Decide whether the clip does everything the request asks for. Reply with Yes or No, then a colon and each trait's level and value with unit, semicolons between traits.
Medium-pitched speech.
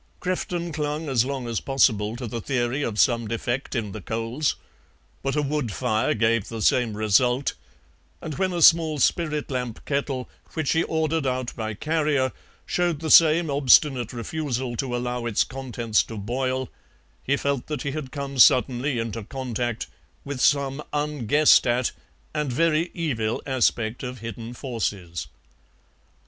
No: low, 130 Hz